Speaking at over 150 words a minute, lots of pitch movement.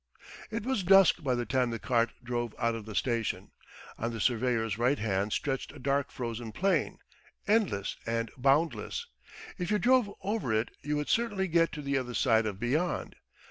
Yes: average, 180 wpm; wide, 7.0 semitones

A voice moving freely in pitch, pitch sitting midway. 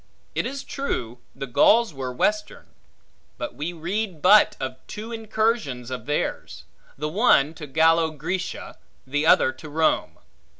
Yes: wide, 7.5 semitones; medium, 160 Hz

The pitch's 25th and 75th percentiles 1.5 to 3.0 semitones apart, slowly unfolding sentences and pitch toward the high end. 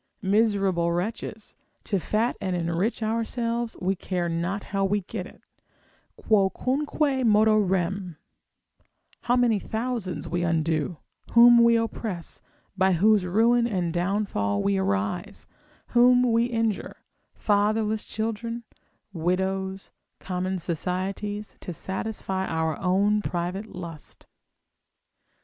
No: average, 4.0 semitones; slow, 110 wpm; high, 195 Hz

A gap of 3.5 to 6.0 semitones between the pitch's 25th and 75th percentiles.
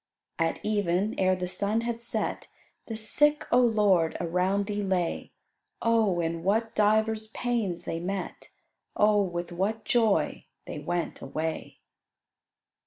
Yes: average, 3.9 semitones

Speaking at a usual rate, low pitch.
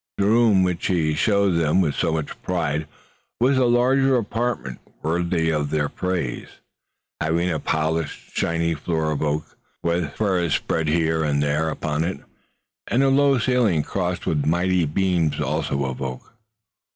Yes: average, 155 wpm; very low, 85 Hz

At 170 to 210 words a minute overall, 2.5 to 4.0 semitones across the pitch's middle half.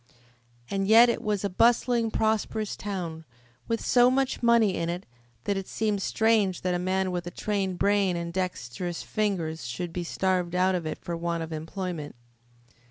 Yes: average, 175 wpm; average, 3.6 semitones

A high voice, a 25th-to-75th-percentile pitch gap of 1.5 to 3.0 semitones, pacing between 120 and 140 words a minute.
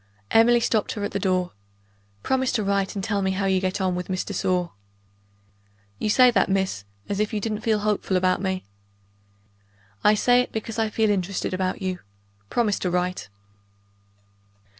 No: high, 200 Hz; average, 2.7 semitones; average, 180 wpm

